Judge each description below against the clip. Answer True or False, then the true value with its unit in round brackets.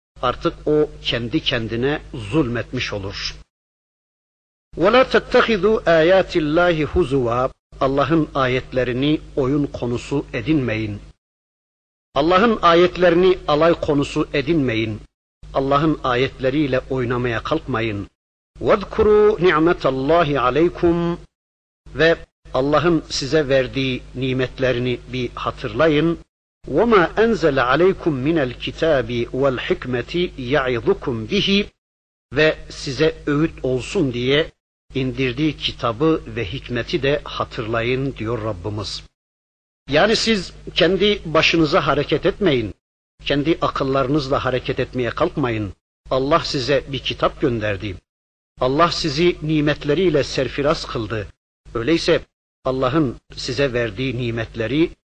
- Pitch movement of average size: True (4.8 semitones)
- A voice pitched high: False (140 Hz)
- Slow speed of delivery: True (90 wpm)